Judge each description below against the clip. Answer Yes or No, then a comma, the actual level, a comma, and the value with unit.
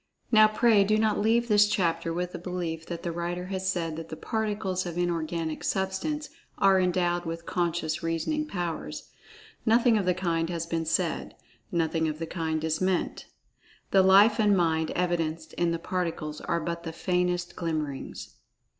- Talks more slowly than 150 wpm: No, average, 170 wpm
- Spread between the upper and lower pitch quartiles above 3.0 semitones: No, narrow, 2.6 semitones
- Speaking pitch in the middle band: Yes, medium, 175 Hz